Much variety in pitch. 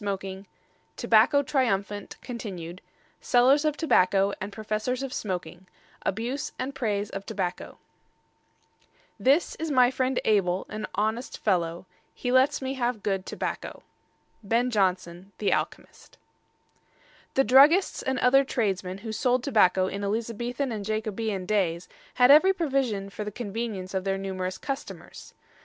No: average, 4.8 semitones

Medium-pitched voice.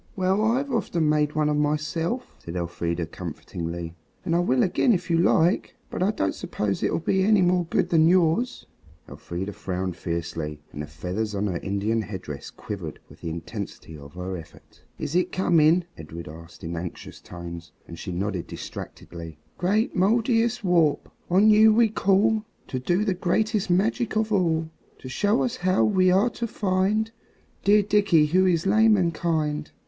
Yes: medium, 165 Hz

